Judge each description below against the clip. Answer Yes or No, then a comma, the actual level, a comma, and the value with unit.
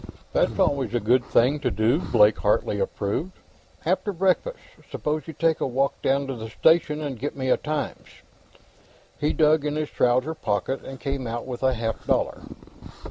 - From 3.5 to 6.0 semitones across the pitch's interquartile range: Yes, average, 4.3 semitones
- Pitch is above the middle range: No, low, 135 Hz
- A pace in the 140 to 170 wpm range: No, average, 180 wpm